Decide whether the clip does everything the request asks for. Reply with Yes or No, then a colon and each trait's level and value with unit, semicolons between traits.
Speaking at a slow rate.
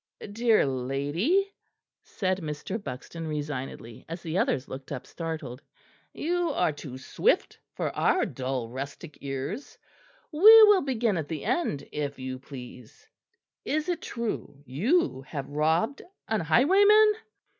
Yes: slow, 130 wpm